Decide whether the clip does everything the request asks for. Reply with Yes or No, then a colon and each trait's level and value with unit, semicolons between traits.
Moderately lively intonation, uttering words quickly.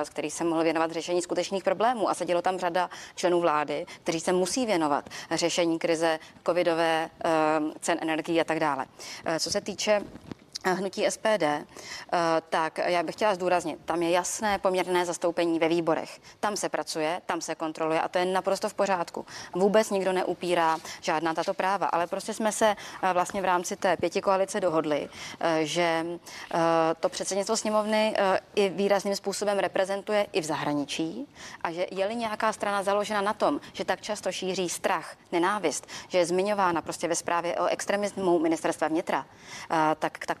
No: average, 3.2 semitones; average, 160 wpm